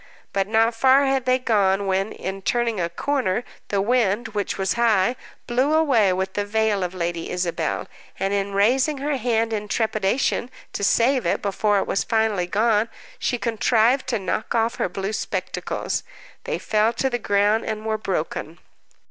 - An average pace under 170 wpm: No, average, 175 wpm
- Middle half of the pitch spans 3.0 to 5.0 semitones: Yes, average, 3.6 semitones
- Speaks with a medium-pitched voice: No, high, 220 Hz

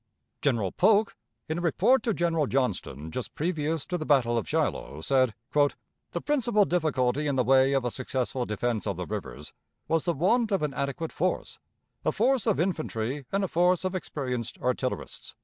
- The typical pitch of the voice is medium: Yes, medium, 145 Hz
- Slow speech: No, average, 180 wpm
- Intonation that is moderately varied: No, wide, 6.1 semitones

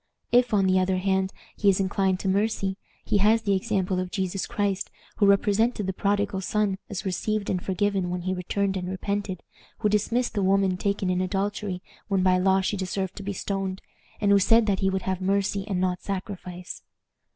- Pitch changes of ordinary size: No, narrow, 1.4 semitones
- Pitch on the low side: No, high, 195 Hz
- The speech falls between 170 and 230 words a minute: Yes, average, 200 wpm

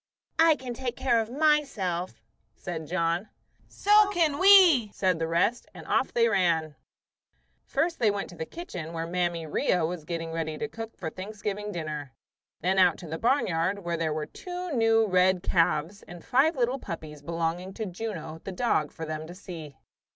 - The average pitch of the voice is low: No, medium, 185 Hz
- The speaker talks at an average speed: Yes, average, 180 wpm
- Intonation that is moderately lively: No, wide, 6.1 semitones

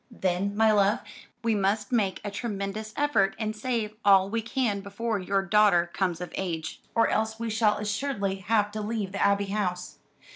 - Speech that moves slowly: No, average, 180 wpm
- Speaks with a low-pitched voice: No, high, 205 Hz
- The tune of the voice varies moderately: No, narrow, 2.1 semitones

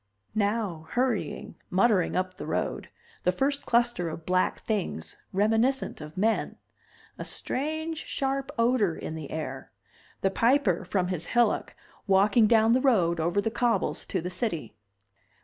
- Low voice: No, high, 205 Hz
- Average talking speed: Yes, average, 145 wpm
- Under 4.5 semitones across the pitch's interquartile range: No, average, 5.1 semitones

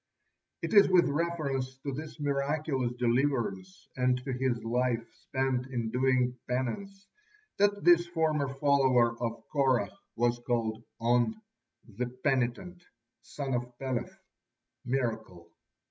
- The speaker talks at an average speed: No, slow, 115 wpm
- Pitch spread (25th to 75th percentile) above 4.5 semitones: No, average, 3.2 semitones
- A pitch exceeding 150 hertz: No, low, 130 Hz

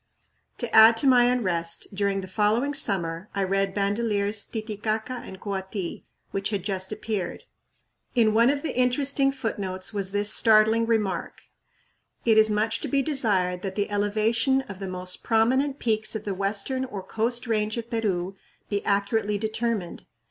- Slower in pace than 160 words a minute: No, average, 165 wpm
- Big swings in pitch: No, average, 2.9 semitones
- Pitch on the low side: No, high, 215 Hz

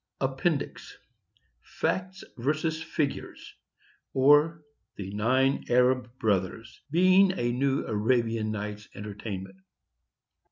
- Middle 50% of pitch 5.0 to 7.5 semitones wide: Yes, wide, 5.4 semitones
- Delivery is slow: Yes, slow, 85 wpm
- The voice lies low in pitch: Yes, low, 125 Hz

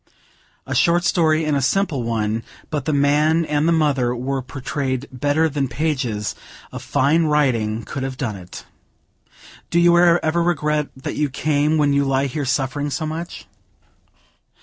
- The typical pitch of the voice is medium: Yes, medium, 145 Hz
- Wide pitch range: No, average, 3.2 semitones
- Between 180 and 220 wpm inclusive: No, average, 160 wpm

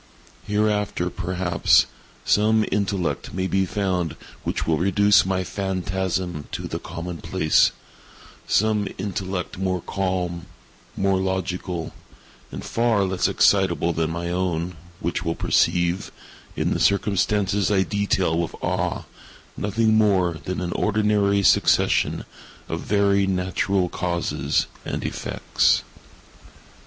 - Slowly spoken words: Yes, slow, 110 wpm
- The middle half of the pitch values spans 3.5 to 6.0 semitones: No, narrow, 2.4 semitones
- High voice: No, very low, 95 Hz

